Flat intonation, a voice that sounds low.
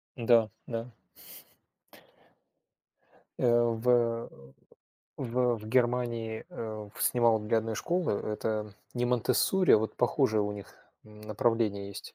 Yes: narrow, 2.2 semitones; low, 115 Hz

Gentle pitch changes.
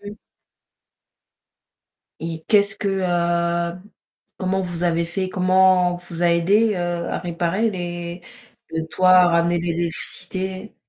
Yes: narrow, 1.6 semitones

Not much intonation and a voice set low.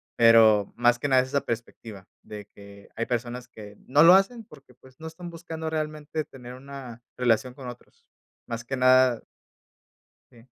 No: average, 4.0 semitones; low, 125 Hz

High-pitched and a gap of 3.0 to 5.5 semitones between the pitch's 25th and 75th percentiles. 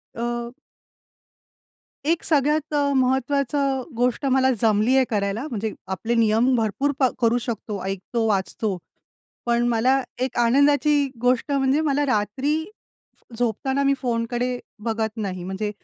Yes: high, 240 Hz; average, 3.6 semitones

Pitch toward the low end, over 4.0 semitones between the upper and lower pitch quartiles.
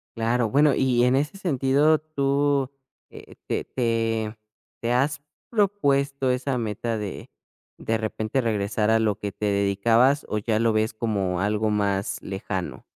Yes: low, 115 Hz; average, 4.4 semitones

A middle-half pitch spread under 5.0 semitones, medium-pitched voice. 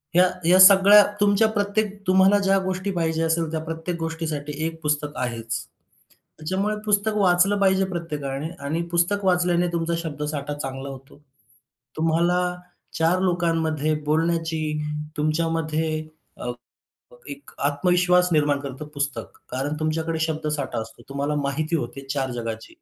Yes: average, 3.4 semitones; medium, 160 Hz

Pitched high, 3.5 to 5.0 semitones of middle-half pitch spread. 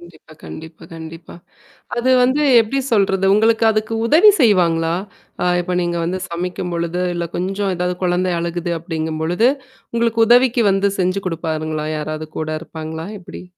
No: medium, 180 Hz; average, 4.2 semitones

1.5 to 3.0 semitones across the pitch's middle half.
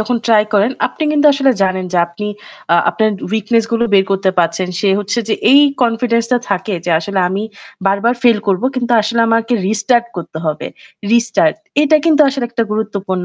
No: average, 3.5 semitones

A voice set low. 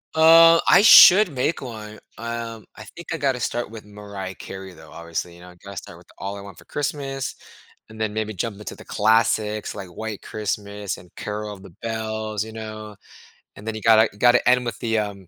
Yes: low, 110 Hz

